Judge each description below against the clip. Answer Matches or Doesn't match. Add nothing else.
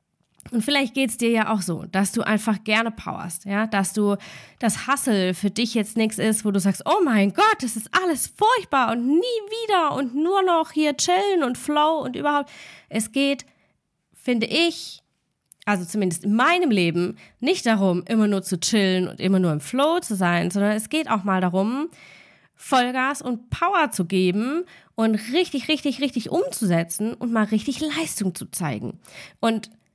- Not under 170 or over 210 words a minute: Matches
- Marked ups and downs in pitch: Matches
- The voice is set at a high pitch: Matches